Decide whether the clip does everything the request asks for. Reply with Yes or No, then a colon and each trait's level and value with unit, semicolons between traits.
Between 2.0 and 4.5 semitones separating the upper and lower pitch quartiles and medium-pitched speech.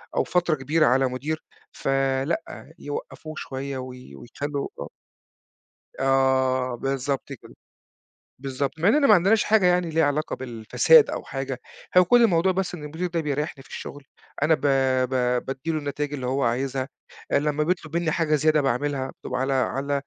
Yes: average, 3.5 semitones; medium, 145 Hz